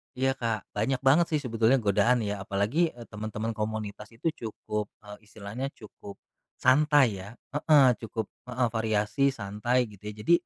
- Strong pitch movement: No, average, 3.6 semitones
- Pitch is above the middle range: No, low, 115 Hz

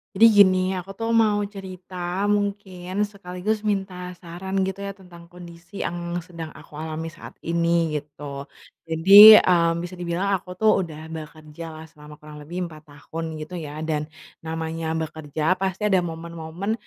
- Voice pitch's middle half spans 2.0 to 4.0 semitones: Yes, average, 2.9 semitones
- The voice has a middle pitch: Yes, medium, 175 Hz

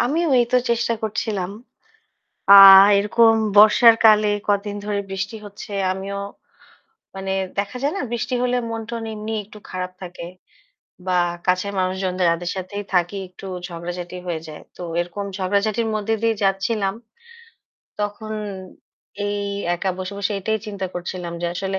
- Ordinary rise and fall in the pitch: Yes, average, 3.0 semitones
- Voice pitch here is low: No, high, 200 Hz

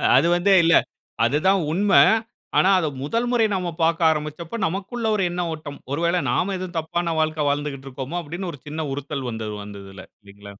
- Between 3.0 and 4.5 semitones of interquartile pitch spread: Yes, average, 4.2 semitones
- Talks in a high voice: No, medium, 160 Hz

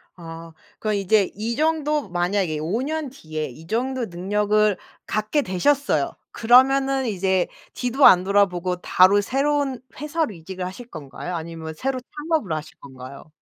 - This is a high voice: Yes, high, 205 Hz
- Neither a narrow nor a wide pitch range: No, wide, 7.2 semitones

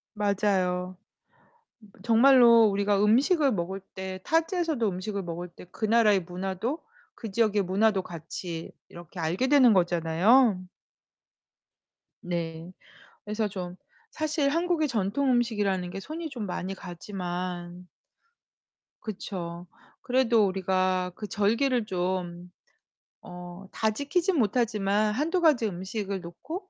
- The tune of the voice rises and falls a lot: No, average, 4.9 semitones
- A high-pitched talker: Yes, high, 200 Hz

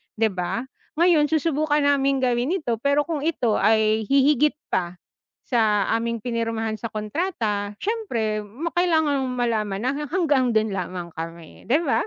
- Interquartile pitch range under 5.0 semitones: No, wide, 5.6 semitones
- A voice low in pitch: No, high, 240 Hz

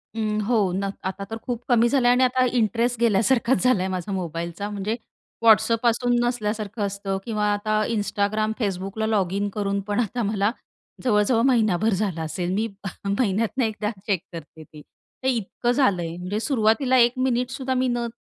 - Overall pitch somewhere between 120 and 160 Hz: No, high, 215 Hz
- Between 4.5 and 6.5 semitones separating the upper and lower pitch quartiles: No, average, 3.4 semitones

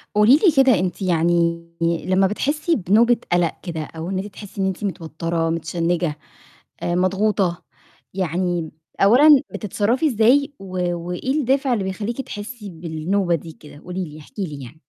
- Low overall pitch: No, medium, 185 Hz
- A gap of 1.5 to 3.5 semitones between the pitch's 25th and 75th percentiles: No, average, 4.2 semitones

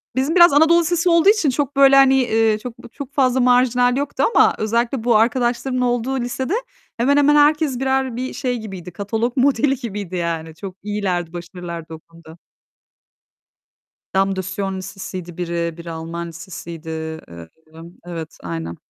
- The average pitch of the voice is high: Yes, high, 225 Hz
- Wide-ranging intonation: Yes, wide, 7.7 semitones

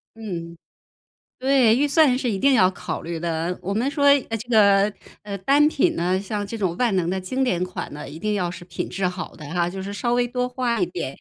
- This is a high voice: Yes, high, 205 Hz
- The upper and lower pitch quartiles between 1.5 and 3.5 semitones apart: No, wide, 5.6 semitones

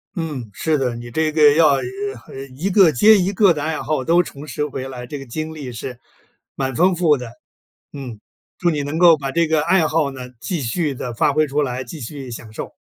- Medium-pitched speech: Yes, medium, 150 Hz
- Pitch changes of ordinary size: Yes, average, 3.7 semitones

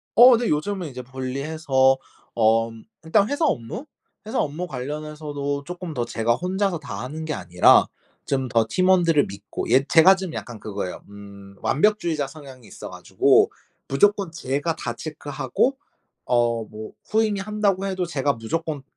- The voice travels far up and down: Yes, wide, 6.9 semitones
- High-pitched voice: No, medium, 145 Hz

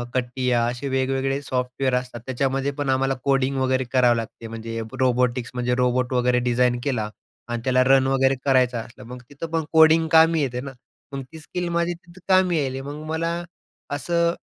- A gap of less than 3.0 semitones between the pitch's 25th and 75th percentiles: Yes, narrow, 2.4 semitones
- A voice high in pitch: No, low, 130 Hz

